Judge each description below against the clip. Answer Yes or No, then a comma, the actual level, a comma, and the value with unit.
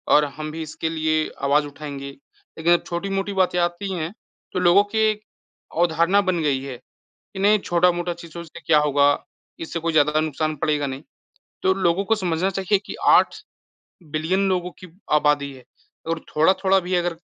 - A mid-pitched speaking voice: Yes, medium, 165 Hz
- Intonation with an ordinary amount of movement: Yes, average, 3.4 semitones